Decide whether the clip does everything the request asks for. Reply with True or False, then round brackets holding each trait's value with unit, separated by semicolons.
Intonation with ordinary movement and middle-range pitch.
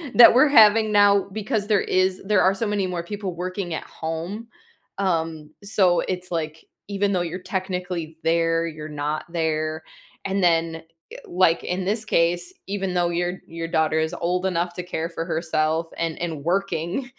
True (3.0 semitones; 175 Hz)